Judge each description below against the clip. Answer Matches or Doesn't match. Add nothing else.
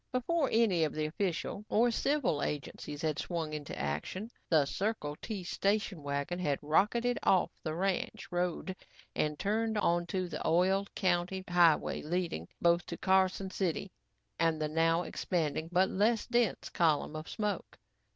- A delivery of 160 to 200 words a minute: Doesn't match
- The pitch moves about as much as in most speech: Matches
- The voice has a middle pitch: Matches